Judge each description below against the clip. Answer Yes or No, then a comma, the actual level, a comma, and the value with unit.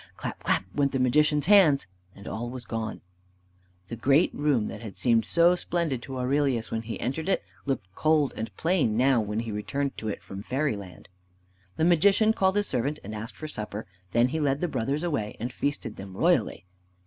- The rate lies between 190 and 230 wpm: Yes, average, 195 wpm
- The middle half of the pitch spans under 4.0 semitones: No, wide, 5.4 semitones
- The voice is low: Yes, low, 130 Hz